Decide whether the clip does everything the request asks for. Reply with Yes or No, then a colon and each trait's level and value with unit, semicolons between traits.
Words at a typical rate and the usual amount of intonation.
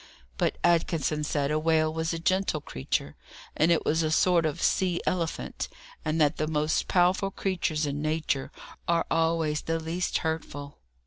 No: average, 165 wpm; narrow, 1.7 semitones